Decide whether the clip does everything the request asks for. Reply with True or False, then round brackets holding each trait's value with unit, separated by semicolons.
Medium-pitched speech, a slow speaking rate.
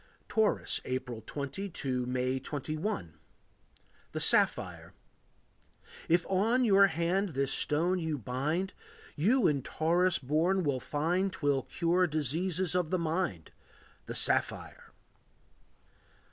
True (160 Hz; 110 wpm)